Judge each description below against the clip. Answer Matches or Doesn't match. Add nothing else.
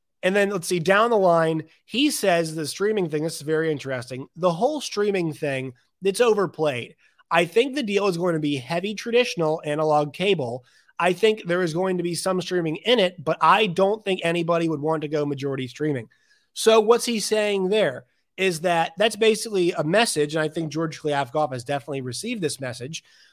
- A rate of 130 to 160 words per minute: Doesn't match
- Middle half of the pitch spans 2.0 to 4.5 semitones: Doesn't match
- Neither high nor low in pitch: Matches